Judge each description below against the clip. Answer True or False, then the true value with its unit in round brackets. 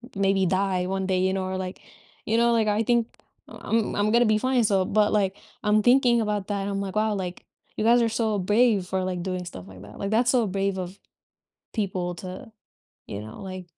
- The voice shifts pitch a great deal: False (3.0 semitones)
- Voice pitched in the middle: False (200 Hz)